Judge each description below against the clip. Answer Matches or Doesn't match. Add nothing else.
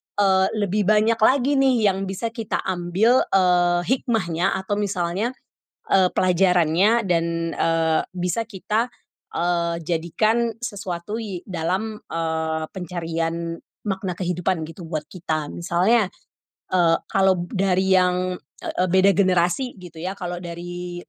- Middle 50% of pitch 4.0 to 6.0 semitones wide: Doesn't match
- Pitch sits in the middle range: Matches